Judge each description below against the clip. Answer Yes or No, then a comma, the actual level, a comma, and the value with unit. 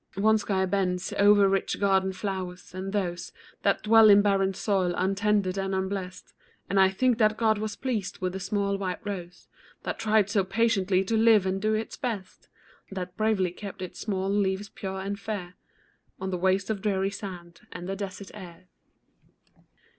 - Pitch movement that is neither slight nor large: No, narrow, 1.8 semitones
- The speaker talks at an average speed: Yes, average, 175 wpm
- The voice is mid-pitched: No, high, 195 Hz